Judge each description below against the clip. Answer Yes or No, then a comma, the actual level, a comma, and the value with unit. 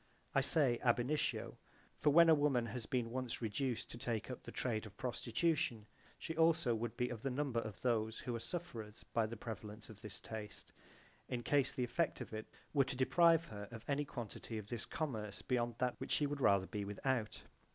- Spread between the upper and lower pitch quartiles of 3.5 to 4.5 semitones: Yes, average, 4.1 semitones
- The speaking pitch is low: Yes, low, 120 Hz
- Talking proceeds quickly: Yes, fast, 210 wpm